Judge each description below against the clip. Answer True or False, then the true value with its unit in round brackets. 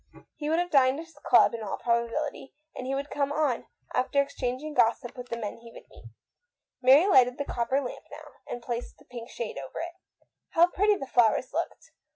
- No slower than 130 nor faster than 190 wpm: False (205 wpm)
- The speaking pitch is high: True (260 Hz)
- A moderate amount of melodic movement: True (3.9 semitones)